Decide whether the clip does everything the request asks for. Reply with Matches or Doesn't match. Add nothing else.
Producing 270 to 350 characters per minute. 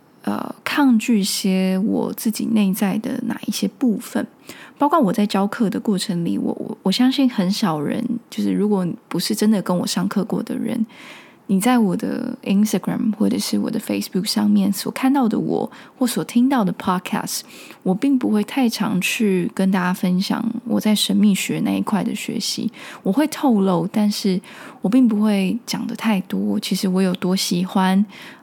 Matches